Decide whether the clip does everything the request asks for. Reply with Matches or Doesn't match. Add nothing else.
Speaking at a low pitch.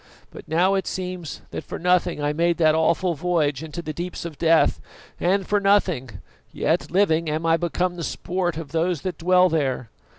Doesn't match